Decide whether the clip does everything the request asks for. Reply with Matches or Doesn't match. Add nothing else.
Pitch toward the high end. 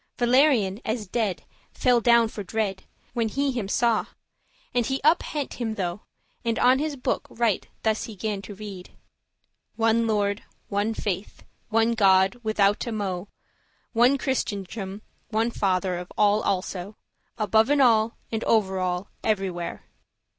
Matches